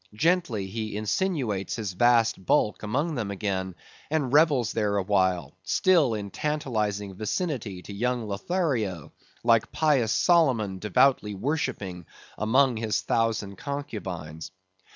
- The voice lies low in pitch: Yes, low, 110 Hz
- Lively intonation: Yes, wide, 5.8 semitones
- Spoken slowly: Yes, slow, 115 wpm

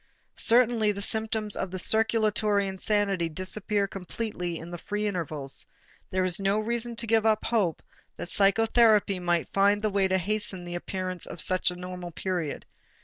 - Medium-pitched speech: No, high, 195 Hz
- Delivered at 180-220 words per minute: No, average, 165 wpm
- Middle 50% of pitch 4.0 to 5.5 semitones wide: No, average, 3.1 semitones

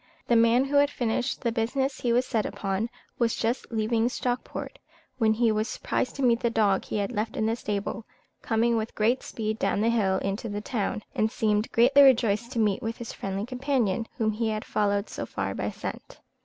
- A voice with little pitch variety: Yes, narrow, 2.3 semitones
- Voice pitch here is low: No, high, 225 Hz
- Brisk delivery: Yes, fast, 210 wpm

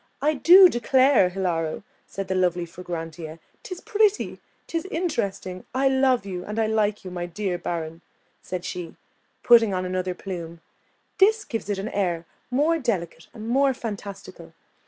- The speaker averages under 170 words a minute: Yes, average, 155 wpm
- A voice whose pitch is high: Yes, high, 195 Hz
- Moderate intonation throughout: No, wide, 6.5 semitones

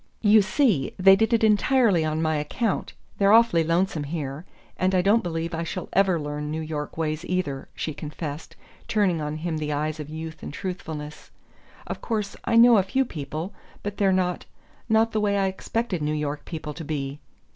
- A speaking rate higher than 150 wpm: Yes, average, 190 wpm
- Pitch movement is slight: No, average, 4.8 semitones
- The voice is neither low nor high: Yes, medium, 170 Hz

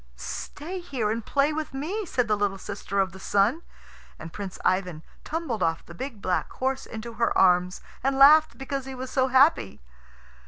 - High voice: Yes, high, 240 Hz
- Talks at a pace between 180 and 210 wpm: Yes, average, 185 wpm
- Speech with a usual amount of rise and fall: No, wide, 6.1 semitones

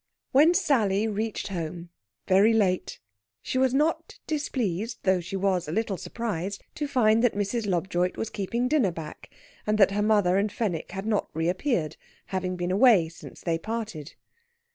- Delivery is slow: No, average, 165 wpm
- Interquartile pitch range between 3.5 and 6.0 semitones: Yes, average, 4.1 semitones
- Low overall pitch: No, high, 200 Hz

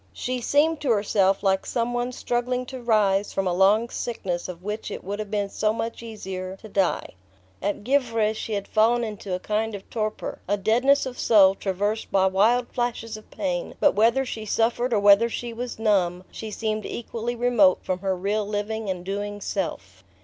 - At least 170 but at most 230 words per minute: Yes, average, 195 wpm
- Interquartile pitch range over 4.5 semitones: No, average, 3.2 semitones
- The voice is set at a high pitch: Yes, high, 215 Hz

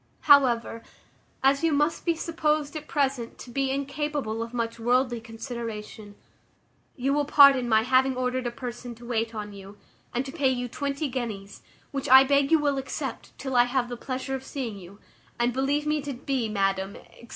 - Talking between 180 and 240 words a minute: Yes, average, 185 wpm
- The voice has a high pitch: Yes, very high, 255 Hz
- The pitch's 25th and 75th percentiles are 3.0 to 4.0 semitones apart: Yes, average, 3.3 semitones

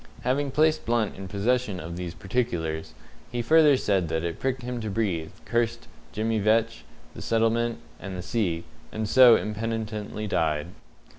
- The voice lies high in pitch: No, low, 110 Hz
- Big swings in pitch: No, average, 4.4 semitones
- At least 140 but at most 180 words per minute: Yes, average, 155 wpm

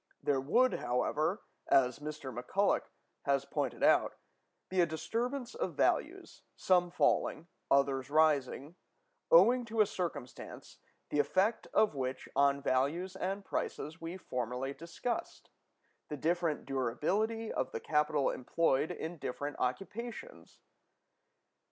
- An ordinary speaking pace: No, slow, 115 wpm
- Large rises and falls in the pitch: Yes, wide, 5.8 semitones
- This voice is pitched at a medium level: Yes, medium, 155 Hz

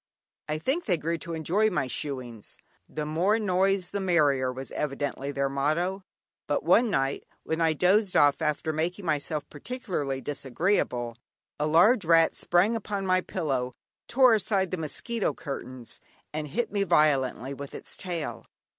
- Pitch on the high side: No, medium, 160 Hz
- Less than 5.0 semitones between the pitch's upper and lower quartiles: No, average, 5.3 semitones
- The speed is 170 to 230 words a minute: No, average, 155 wpm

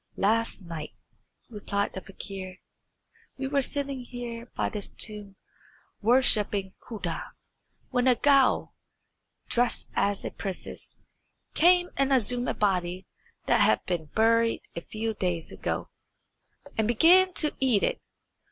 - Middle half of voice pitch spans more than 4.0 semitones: Yes, average, 4.7 semitones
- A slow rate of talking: Yes, slow, 125 wpm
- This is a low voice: No, high, 225 Hz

